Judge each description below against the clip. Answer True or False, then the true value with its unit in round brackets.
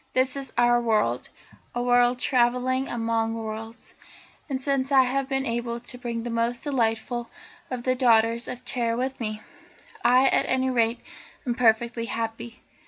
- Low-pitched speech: False (240 Hz)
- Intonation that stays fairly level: True (2.0 semitones)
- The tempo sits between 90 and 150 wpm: False (160 wpm)